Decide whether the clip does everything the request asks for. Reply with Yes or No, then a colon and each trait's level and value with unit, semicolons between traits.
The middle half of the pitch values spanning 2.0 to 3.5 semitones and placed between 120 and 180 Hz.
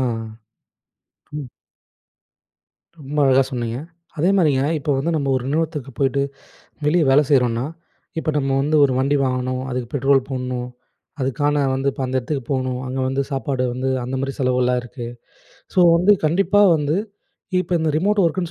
Yes: average, 2.8 semitones; low, 135 Hz